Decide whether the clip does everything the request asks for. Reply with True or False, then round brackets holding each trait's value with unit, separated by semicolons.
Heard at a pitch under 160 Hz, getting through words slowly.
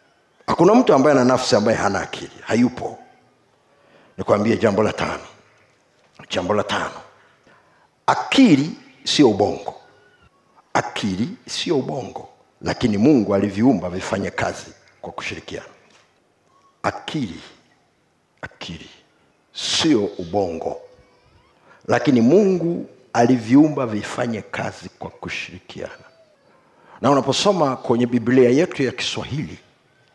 True (135 Hz; 95 wpm)